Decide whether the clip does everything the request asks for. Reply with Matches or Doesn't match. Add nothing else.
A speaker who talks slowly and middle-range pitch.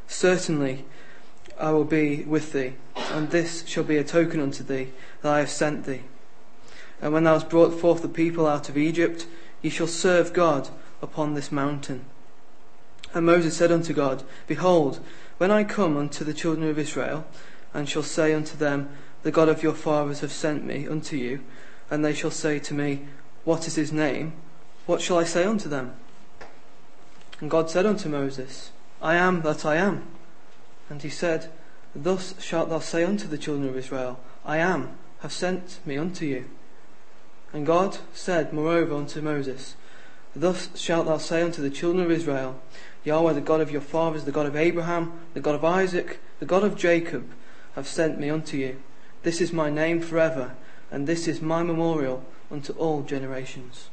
Doesn't match